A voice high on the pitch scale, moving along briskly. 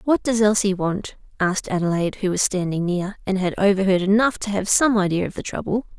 Yes: high, 195 Hz; fast, 210 wpm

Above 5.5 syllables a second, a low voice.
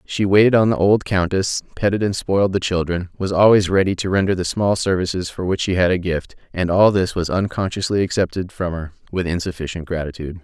Yes: 5.8 syllables/s; very low, 95 Hz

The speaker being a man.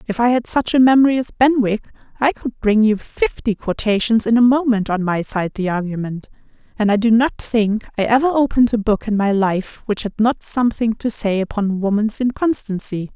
No: female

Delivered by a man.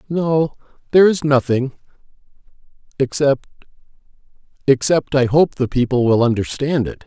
Yes: male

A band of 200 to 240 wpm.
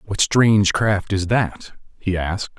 No: average, 165 wpm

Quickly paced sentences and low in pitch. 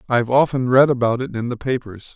Yes: fast, 225 wpm; low, 125 Hz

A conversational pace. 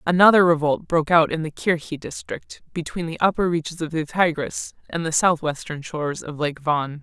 Yes: average, 190 wpm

